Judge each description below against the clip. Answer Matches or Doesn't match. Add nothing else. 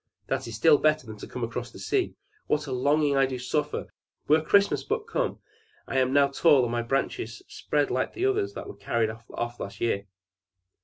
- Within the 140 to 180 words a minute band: Doesn't match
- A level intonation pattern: Doesn't match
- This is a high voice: Doesn't match